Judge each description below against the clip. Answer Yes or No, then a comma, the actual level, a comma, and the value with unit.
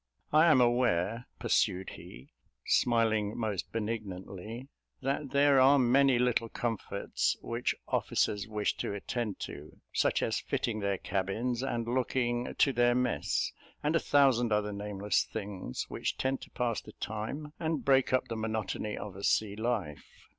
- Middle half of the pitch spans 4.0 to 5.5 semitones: No, average, 3.6 semitones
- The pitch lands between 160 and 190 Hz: No, low, 115 Hz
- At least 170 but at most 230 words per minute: No, average, 150 wpm